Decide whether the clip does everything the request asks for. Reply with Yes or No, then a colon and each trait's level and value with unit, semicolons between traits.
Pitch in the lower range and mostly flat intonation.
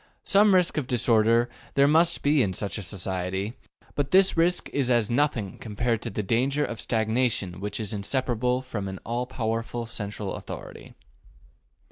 No: low, 115 Hz; average, 4.6 semitones